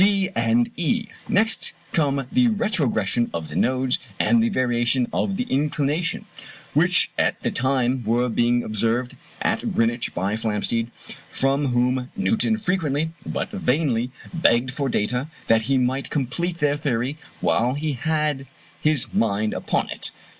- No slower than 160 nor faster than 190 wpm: No, average, 145 wpm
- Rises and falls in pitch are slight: No, average, 5.0 semitones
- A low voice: Yes, low, 130 Hz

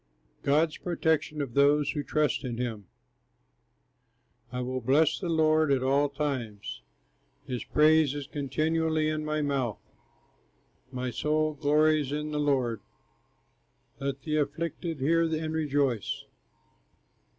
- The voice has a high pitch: No, medium, 145 Hz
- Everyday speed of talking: No, slow, 120 wpm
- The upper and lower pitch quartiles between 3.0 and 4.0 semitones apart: No, narrow, 2.6 semitones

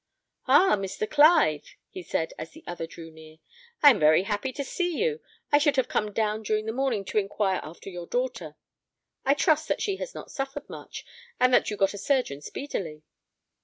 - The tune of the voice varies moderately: No, wide, 8.1 semitones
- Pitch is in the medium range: No, high, 215 Hz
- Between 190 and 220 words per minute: Yes, average, 200 wpm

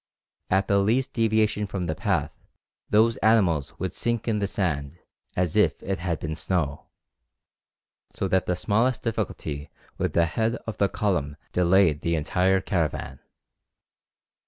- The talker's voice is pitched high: No, very low, 95 Hz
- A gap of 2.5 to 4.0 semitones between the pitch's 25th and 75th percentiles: No, average, 4.4 semitones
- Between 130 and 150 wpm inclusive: Yes, average, 145 wpm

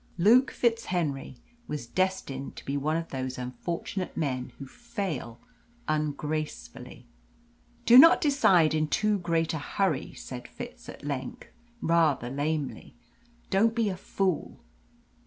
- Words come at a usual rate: No, slow, 125 wpm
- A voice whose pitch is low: No, medium, 160 Hz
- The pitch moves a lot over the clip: Yes, wide, 5.8 semitones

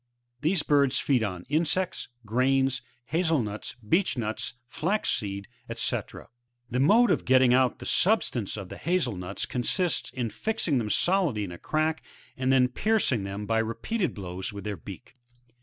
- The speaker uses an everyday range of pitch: No, wide, 7.2 semitones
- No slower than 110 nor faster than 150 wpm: No, average, 165 wpm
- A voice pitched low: Yes, low, 130 Hz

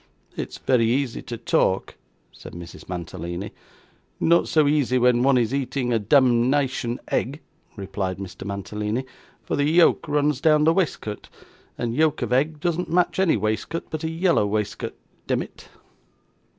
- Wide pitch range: Yes, wide, 6.2 semitones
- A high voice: No, low, 130 Hz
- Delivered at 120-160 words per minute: Yes, average, 150 wpm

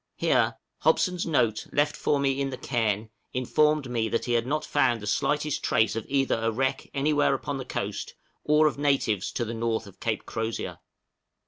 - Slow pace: No, average, 190 wpm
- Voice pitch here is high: No, low, 130 Hz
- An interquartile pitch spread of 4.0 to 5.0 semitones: Yes, average, 4.3 semitones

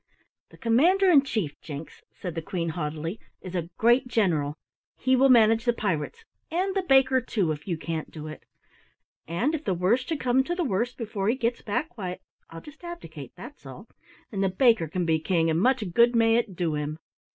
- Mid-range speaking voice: No, high, 215 Hz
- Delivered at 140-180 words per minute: No, fast, 205 wpm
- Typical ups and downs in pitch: No, wide, 7.6 semitones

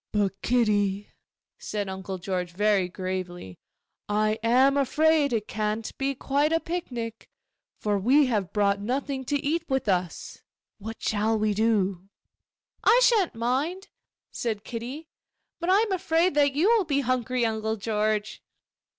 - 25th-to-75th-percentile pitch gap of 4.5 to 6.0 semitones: Yes, wide, 5.5 semitones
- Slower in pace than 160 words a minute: Yes, average, 140 wpm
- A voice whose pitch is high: Yes, high, 225 Hz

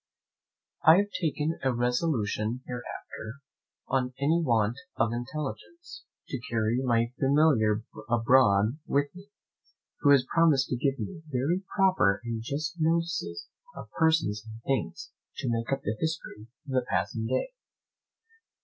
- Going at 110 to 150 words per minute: Yes, slow, 135 wpm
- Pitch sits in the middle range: No, low, 130 Hz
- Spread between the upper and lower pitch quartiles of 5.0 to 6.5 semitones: Yes, wide, 5.5 semitones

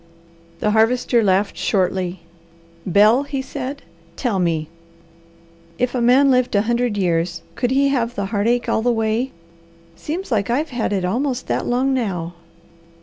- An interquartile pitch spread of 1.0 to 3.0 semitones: No, average, 4.3 semitones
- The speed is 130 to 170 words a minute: Yes, average, 150 wpm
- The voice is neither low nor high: No, high, 235 Hz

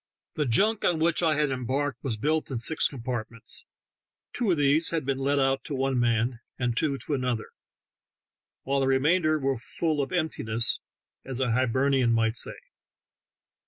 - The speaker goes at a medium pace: Yes, average, 170 wpm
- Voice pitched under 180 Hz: Yes, low, 135 Hz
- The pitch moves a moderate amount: Yes, average, 3.8 semitones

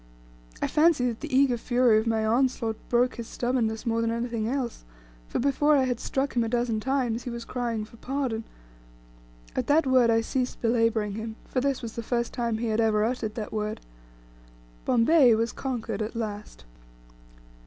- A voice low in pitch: No, high, 235 Hz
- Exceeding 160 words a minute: Yes, average, 185 wpm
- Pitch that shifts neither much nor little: No, narrow, 2.3 semitones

